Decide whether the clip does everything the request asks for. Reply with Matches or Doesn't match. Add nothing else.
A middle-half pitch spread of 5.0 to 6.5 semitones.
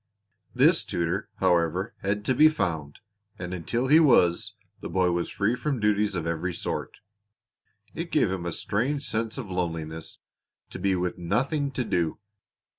Matches